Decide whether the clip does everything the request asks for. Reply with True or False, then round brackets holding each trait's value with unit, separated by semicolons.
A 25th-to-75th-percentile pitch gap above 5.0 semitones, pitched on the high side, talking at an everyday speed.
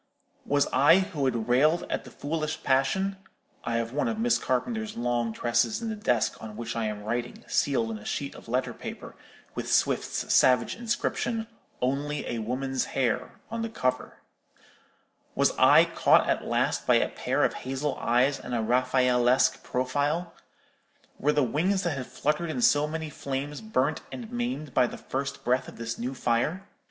False (5.5 semitones; 135 Hz; 170 wpm)